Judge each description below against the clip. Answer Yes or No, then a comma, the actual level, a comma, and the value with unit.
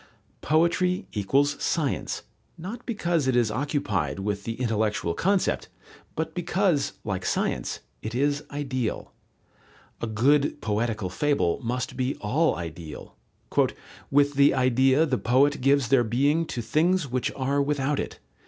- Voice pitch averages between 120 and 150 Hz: Yes, low, 135 Hz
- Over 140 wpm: No, slow, 135 wpm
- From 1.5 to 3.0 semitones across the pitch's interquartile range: No, average, 4.7 semitones